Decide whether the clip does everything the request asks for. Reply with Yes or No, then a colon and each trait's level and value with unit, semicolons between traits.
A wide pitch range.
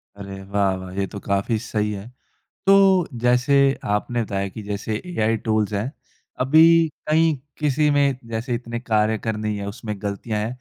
No: average, 3.8 semitones